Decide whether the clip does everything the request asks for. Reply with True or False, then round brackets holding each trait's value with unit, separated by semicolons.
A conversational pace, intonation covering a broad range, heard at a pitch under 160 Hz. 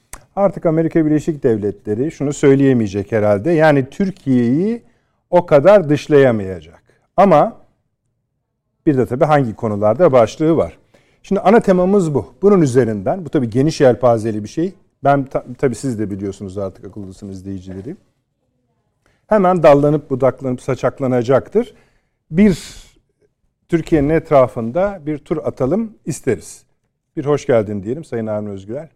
True (120 wpm; 6.0 semitones; 135 Hz)